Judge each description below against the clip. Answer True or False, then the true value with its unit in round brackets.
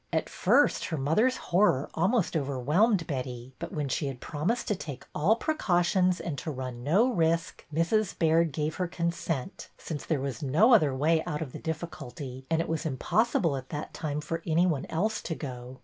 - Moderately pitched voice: True (160 Hz)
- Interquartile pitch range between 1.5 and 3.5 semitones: False (4.2 semitones)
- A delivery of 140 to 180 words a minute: False (190 wpm)